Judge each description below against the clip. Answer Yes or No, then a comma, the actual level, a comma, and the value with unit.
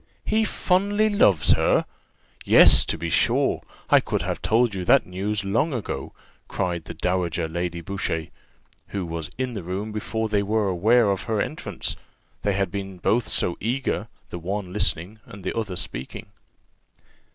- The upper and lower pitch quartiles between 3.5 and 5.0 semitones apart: Yes, average, 3.8 semitones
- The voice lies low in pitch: Yes, low, 100 Hz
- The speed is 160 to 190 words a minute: Yes, average, 165 wpm